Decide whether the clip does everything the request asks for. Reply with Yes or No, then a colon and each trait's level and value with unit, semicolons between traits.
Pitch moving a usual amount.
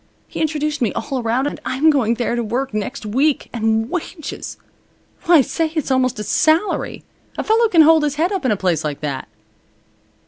No: wide, 5.7 semitones